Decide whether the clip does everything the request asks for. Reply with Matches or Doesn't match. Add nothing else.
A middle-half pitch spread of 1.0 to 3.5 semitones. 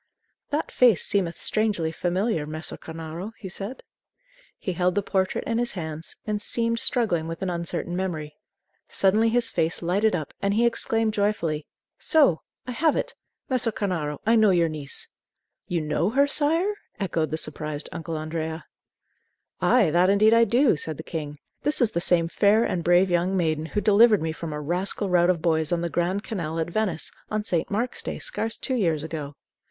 Doesn't match